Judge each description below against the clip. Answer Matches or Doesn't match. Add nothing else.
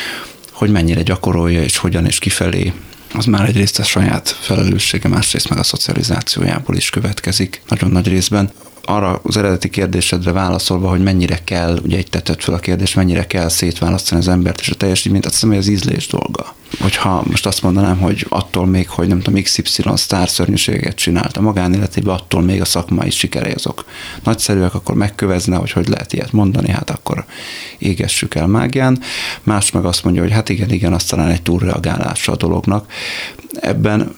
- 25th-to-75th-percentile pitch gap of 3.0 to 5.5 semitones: Doesn't match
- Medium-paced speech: Doesn't match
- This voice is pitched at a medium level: Doesn't match